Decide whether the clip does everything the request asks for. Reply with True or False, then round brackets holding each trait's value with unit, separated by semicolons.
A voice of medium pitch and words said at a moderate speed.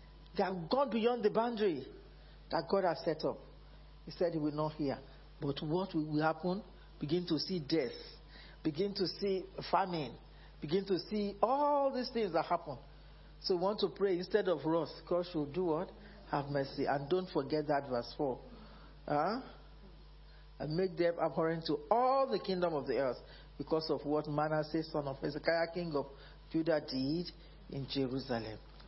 True (165 Hz; 170 wpm)